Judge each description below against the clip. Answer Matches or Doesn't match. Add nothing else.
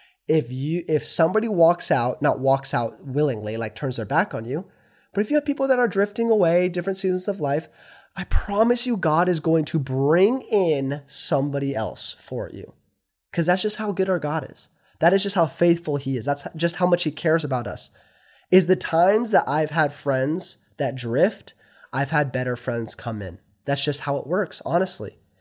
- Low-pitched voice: Doesn't match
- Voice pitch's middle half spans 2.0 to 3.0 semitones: Doesn't match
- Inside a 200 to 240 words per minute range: Matches